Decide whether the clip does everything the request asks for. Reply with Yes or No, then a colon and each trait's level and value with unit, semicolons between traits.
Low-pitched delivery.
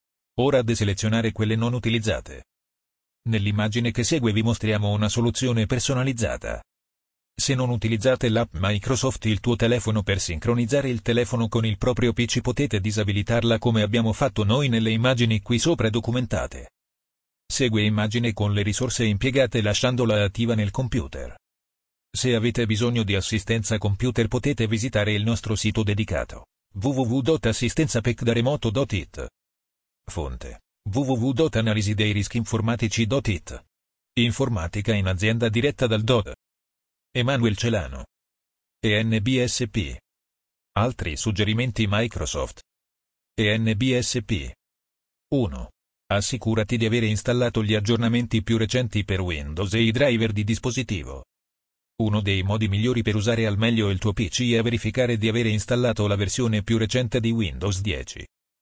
Yes: low, 110 Hz